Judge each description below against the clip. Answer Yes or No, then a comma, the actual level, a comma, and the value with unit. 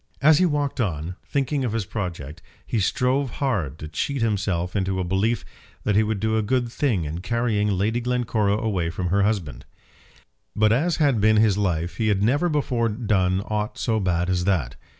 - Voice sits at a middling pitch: No, low, 105 Hz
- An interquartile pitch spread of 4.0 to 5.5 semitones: Yes, average, 4.5 semitones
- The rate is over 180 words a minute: Yes, average, 190 wpm